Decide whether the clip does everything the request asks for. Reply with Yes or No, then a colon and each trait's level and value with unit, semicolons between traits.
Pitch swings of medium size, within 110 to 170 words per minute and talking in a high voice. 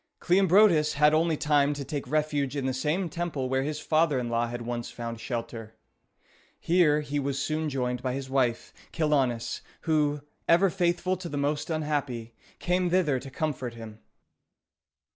No: average, 3.8 semitones; average, 160 wpm; medium, 145 Hz